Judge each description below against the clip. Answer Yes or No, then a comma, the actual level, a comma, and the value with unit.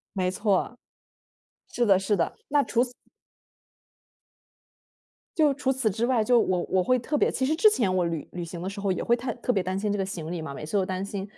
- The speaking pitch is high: Yes, high, 200 Hz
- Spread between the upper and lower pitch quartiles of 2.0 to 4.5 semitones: No, average, 4.9 semitones